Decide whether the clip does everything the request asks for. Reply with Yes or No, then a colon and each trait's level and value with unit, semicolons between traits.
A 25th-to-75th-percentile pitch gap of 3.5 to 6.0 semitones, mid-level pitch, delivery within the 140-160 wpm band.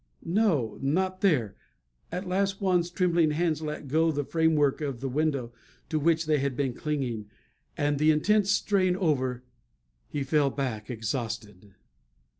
Yes: average, 4.7 semitones; medium, 150 Hz; average, 145 wpm